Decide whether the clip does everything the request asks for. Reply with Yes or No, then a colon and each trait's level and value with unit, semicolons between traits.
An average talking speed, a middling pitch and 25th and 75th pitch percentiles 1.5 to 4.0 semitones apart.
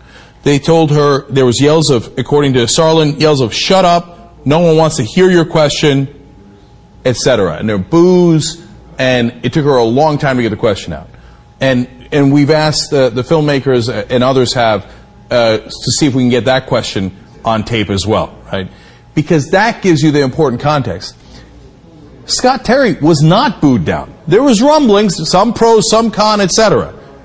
No: average, 185 wpm; medium, 145 Hz; average, 5.0 semitones